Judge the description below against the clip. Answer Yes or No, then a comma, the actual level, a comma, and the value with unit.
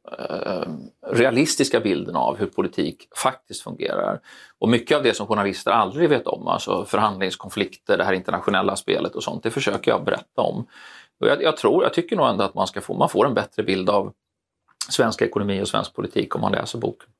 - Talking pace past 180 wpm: Yes, average, 190 wpm